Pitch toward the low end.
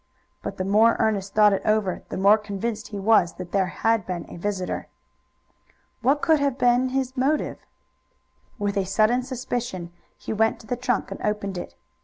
No: high, 215 Hz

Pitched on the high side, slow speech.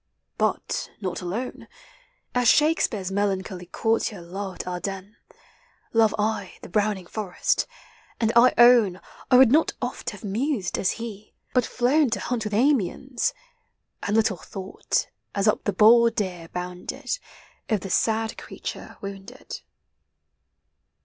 Yes: high, 215 Hz; slow, 130 wpm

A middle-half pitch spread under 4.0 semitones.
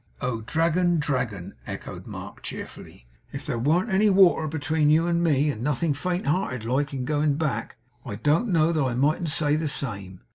No: average, 4.3 semitones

